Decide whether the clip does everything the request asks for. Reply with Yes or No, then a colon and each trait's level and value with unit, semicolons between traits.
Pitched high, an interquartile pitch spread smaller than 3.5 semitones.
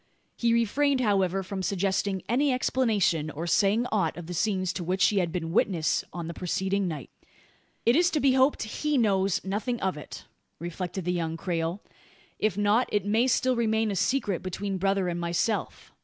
No: high, 195 Hz; average, 4.1 semitones